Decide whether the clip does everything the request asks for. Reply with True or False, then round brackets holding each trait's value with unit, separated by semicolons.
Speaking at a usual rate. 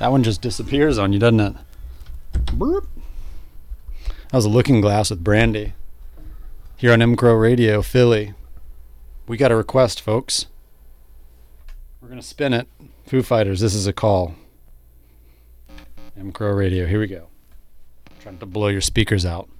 True (145 wpm)